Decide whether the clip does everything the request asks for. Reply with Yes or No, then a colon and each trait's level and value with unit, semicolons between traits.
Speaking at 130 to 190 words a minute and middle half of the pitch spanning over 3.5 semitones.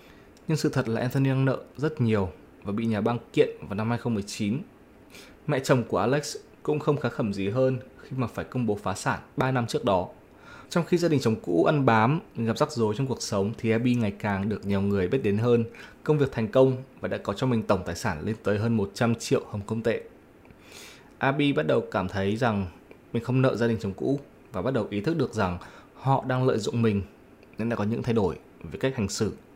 No: average, 240 wpm; average, 4.3 semitones